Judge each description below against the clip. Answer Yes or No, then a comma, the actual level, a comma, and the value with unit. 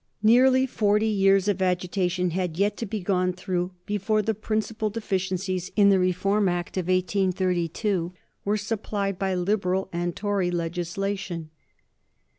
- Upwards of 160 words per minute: No, slow, 135 wpm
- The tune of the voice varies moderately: No, narrow, 2.3 semitones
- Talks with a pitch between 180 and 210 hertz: Yes, high, 190 Hz